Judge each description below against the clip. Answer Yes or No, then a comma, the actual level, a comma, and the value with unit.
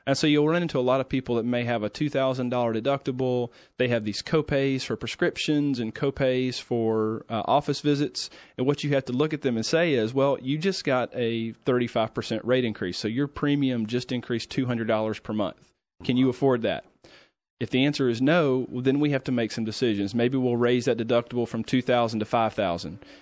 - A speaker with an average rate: No, fast, 225 wpm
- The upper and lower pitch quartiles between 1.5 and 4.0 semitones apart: Yes, average, 2.9 semitones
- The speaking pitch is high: No, low, 125 Hz